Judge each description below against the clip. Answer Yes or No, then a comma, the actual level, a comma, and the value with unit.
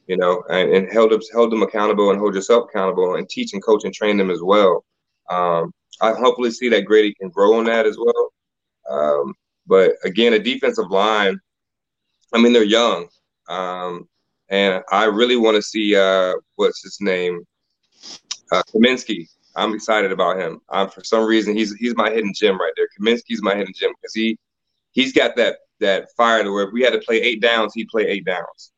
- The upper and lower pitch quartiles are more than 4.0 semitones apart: Yes, average, 4.5 semitones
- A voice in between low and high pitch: No, low, 110 Hz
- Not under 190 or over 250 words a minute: Yes, average, 200 wpm